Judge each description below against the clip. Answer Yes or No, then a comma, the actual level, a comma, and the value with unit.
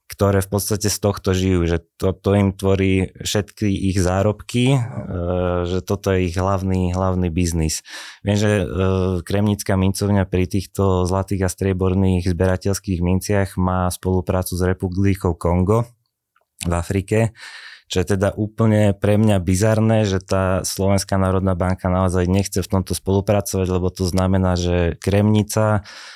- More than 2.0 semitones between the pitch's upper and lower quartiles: No, narrow, 1.6 semitones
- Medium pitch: No, very low, 95 Hz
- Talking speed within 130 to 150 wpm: Yes, average, 140 wpm